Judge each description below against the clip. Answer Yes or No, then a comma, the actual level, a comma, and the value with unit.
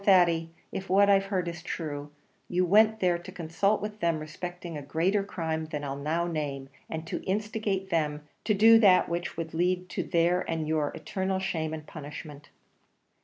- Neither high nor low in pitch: Yes, medium, 170 Hz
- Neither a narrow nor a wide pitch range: Yes, average, 3.4 semitones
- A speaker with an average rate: Yes, average, 180 wpm